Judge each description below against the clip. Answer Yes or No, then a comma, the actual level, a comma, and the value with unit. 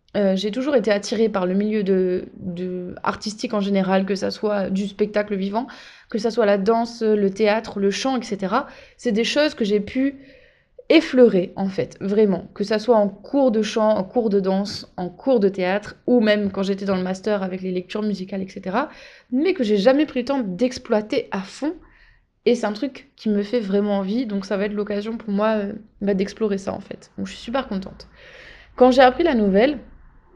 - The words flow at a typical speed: Yes, average, 210 wpm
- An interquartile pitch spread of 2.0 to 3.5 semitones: No, average, 3.9 semitones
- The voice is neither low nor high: No, high, 210 Hz